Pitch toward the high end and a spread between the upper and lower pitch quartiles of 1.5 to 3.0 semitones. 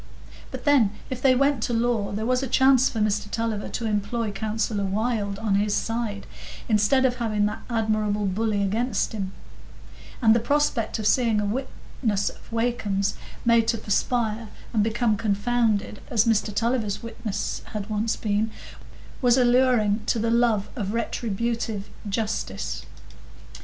Yes: high, 220 Hz; narrow, 2.4 semitones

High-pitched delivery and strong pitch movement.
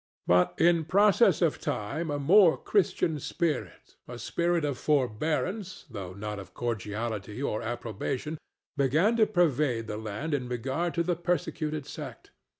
No: medium, 145 Hz; wide, 6.9 semitones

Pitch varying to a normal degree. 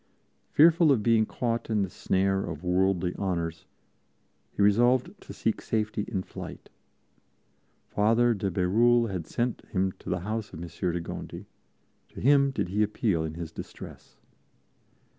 Yes: average, 4.5 semitones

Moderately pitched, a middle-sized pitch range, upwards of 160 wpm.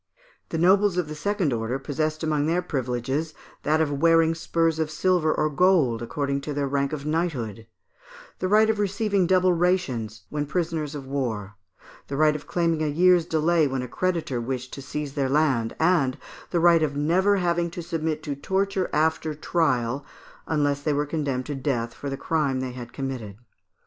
Yes: medium, 150 Hz; average, 3.9 semitones; average, 180 wpm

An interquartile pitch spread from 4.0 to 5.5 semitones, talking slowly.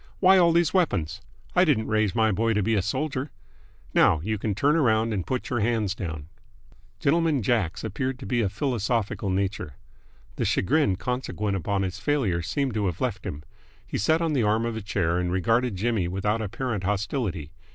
No: average, 5.1 semitones; average, 190 wpm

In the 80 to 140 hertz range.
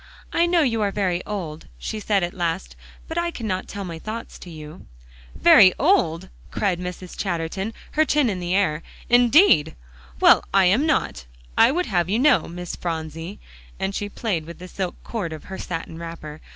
No: medium, 185 Hz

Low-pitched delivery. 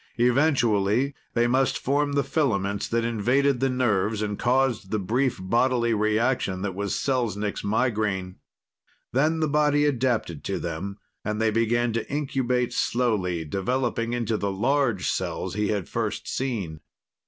Yes: low, 115 Hz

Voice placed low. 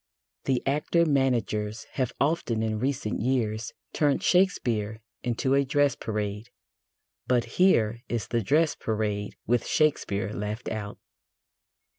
Yes: low, 120 Hz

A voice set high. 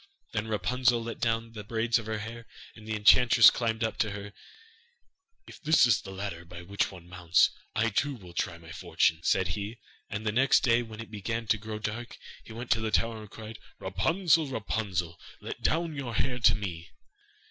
No: low, 110 Hz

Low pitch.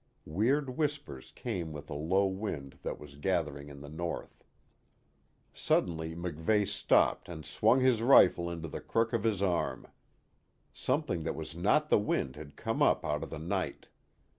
Yes: very low, 85 Hz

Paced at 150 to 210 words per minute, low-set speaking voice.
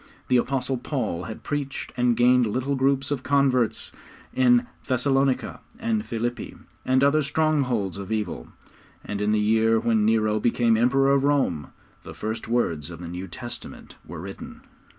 Yes: average, 155 wpm; low, 120 Hz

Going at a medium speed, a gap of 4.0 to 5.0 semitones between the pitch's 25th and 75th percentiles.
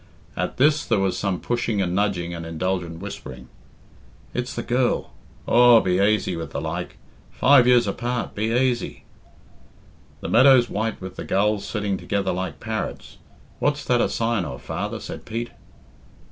Yes: average, 160 wpm; average, 4.6 semitones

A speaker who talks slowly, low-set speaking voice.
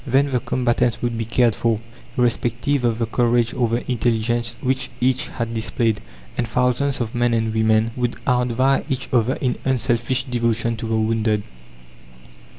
No: average, 160 wpm; low, 120 Hz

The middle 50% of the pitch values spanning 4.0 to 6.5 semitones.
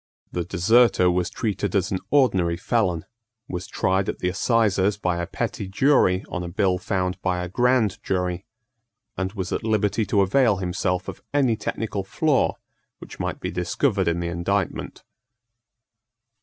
No: average, 3.3 semitones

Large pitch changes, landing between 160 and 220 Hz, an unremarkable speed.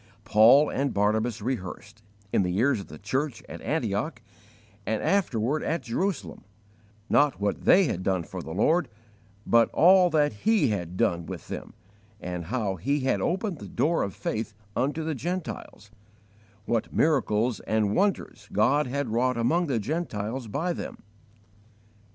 No: wide, 6.6 semitones; low, 120 Hz; average, 150 wpm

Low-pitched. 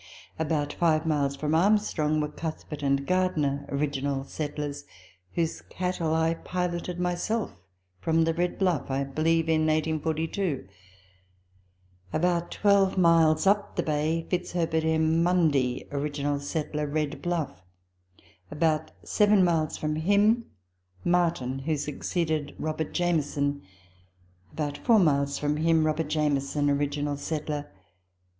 No: medium, 155 Hz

